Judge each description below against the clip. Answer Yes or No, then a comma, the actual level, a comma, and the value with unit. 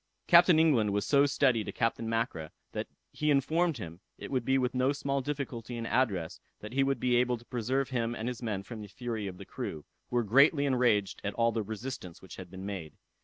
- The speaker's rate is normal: No, fast, 220 wpm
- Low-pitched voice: Yes, low, 120 Hz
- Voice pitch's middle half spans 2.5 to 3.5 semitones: No, average, 4.3 semitones